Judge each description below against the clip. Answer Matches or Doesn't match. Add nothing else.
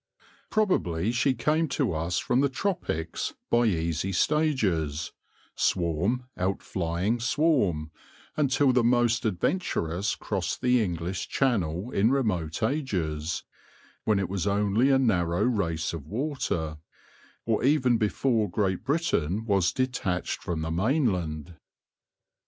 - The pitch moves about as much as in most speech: Doesn't match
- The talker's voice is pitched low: Matches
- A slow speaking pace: Matches